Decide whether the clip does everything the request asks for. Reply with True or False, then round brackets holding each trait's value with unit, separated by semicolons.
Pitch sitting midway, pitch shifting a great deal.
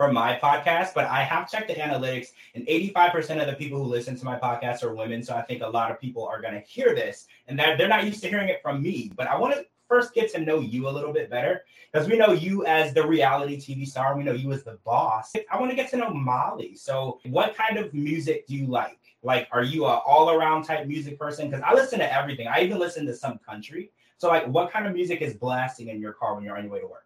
True (150 Hz; 5.8 semitones)